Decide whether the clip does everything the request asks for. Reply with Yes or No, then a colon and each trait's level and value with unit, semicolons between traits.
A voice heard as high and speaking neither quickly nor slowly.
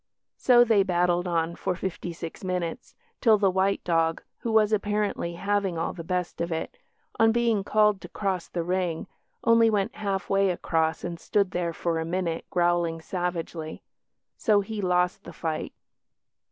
No: medium, 180 Hz; average, 165 wpm